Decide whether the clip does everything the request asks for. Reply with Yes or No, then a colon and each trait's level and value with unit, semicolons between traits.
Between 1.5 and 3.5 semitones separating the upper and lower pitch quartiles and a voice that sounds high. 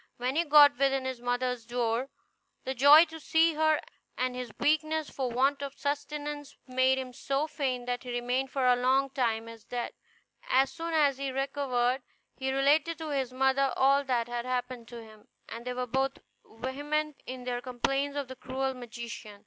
Yes: narrow, 2.4 semitones; very high, 265 Hz